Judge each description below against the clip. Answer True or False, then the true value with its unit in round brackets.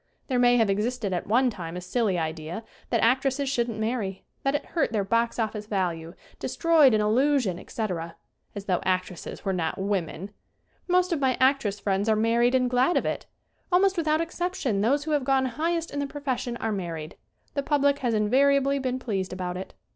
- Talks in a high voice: True (235 Hz)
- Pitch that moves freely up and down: True (6.0 semitones)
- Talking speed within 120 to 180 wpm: False (195 wpm)